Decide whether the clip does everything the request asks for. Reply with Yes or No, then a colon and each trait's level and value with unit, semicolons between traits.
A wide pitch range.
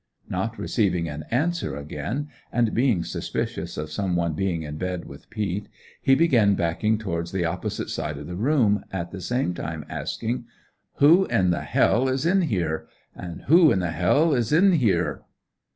Yes: wide, 7.4 semitones